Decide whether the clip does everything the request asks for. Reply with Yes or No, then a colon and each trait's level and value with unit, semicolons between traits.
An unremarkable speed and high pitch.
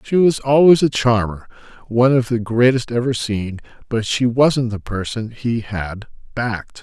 No: average, 165 wpm; low, 120 Hz